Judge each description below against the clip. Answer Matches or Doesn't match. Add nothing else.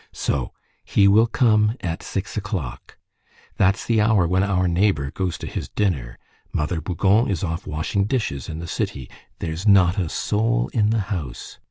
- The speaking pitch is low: Matches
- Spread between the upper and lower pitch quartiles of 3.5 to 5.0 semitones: Matches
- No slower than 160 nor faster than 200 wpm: Matches